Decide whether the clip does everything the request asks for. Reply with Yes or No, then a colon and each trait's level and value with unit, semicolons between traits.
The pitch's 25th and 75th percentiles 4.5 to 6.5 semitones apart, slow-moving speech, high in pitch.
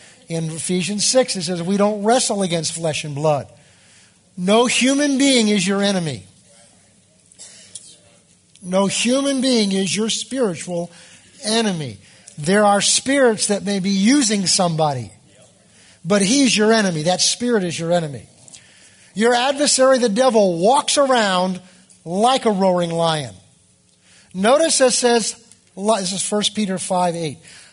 Yes: average, 5.3 semitones; slow, 130 wpm; high, 195 Hz